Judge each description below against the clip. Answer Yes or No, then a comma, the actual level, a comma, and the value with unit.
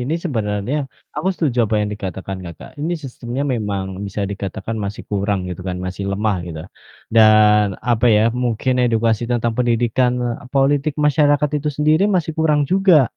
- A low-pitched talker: Yes, low, 115 Hz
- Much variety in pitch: Yes, wide, 5.9 semitones